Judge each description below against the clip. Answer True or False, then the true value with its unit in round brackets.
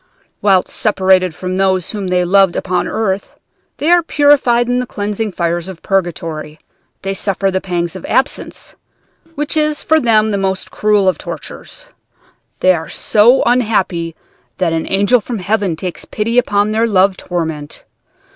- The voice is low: False (195 Hz)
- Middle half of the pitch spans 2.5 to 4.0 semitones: True (3.6 semitones)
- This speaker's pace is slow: False (155 wpm)